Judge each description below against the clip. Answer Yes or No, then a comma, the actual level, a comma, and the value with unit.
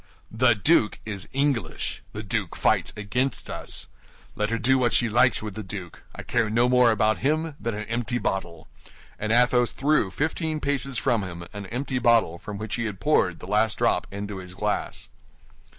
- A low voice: Yes, low, 115 Hz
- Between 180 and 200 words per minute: Yes, average, 185 wpm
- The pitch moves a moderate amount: Yes, average, 3.6 semitones